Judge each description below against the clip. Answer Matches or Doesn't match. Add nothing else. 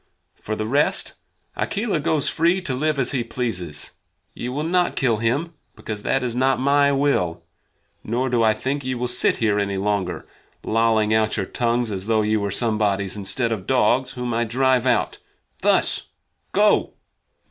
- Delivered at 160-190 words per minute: Matches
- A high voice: Doesn't match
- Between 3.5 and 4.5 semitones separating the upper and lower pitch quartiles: Matches